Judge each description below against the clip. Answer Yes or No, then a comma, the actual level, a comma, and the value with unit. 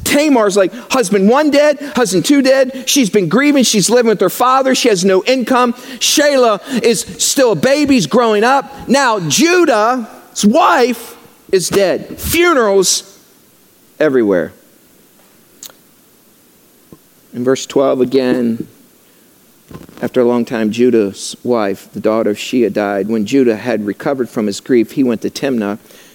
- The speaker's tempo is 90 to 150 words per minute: Yes, average, 140 wpm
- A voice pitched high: Yes, high, 225 Hz